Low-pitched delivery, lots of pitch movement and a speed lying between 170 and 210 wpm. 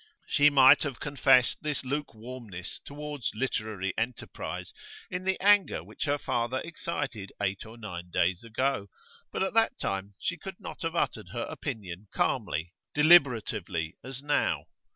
No: low, 125 Hz; wide, 6.4 semitones; average, 145 wpm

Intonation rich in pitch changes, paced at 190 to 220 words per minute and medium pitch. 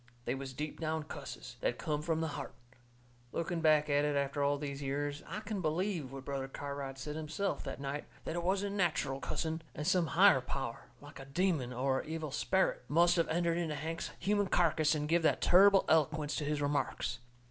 No: average, 3.2 semitones; average, 200 wpm; medium, 155 Hz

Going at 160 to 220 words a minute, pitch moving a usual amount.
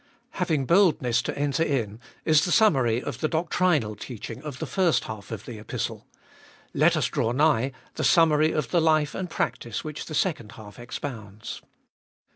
No: average, 175 wpm; wide, 5.7 semitones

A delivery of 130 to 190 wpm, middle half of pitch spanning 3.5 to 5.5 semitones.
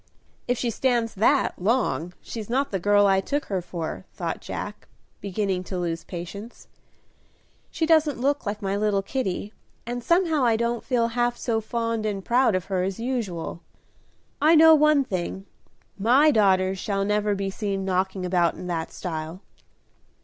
Yes: average, 165 wpm; average, 4.5 semitones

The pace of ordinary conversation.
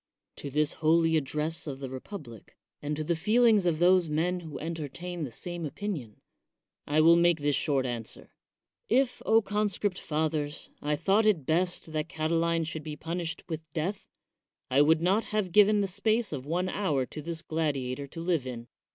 Yes: average, 175 wpm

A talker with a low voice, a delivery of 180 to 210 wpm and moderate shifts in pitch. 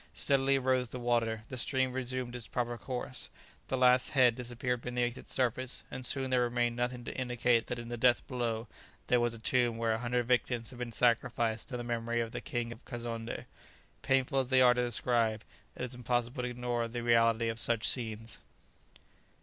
No: low, 120 Hz; average, 200 wpm; narrow, 1.2 semitones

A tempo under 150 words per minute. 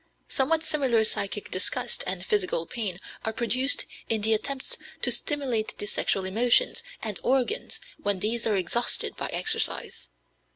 Yes: average, 140 wpm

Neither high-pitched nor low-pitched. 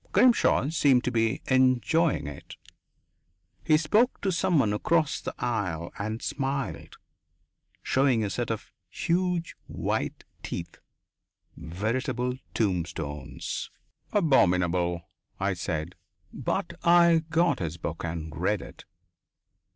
No: low, 125 Hz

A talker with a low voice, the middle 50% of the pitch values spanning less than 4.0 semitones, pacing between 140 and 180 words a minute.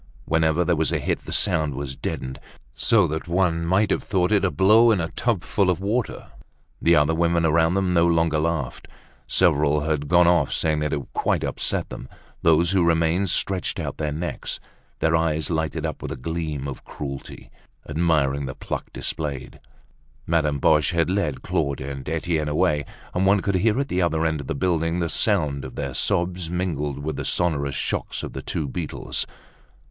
No: very low, 80 Hz; average, 2.9 semitones; average, 190 wpm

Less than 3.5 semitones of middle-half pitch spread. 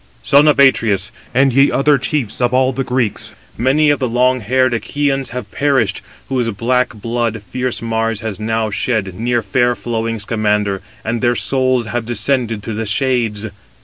Yes: narrow, 2.6 semitones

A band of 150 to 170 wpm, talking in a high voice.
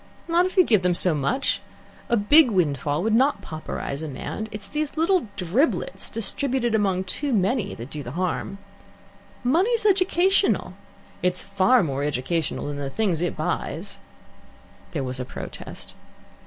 Yes: average, 155 wpm; high, 200 Hz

